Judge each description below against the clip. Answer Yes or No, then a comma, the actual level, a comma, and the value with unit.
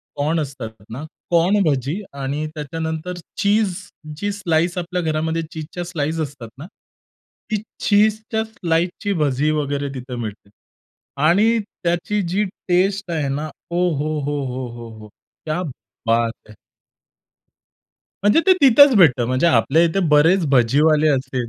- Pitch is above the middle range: No, medium, 160 Hz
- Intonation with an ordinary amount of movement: Yes, average, 4.7 semitones